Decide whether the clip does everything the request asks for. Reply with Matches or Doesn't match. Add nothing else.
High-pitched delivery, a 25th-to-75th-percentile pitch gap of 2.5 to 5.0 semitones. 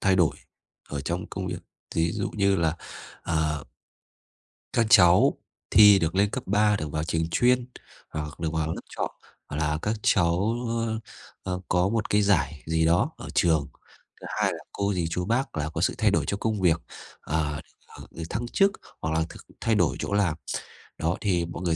Doesn't match